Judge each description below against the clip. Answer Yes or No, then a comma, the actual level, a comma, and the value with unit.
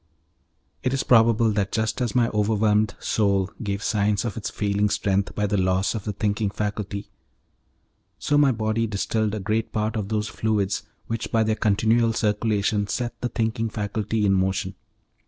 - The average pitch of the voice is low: Yes, low, 105 Hz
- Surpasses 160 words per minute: Yes, average, 170 wpm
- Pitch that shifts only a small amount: Yes, narrow, 1.7 semitones